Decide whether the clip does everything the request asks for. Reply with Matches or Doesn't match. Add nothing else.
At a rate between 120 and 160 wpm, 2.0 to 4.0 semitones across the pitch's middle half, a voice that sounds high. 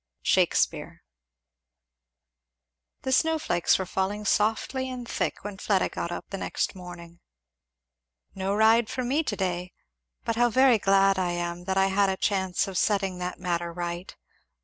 Matches